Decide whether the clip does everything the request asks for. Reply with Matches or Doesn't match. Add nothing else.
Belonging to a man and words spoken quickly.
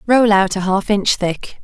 Doesn't match